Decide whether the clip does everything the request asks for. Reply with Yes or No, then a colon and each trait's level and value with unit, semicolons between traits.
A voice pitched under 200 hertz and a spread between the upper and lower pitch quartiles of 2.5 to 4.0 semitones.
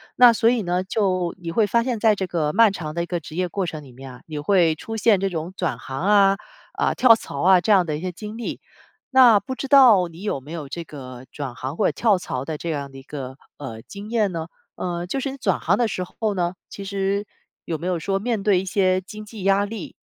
No: medium, 185 Hz; average, 4.6 semitones